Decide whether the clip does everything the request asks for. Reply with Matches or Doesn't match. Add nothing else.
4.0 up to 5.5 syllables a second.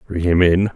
Matches